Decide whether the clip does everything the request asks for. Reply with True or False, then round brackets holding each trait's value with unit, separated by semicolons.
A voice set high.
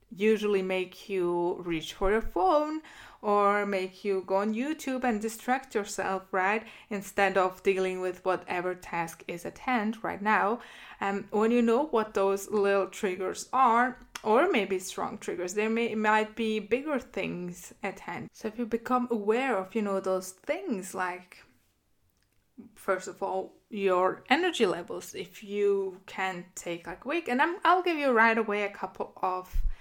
True (205 Hz)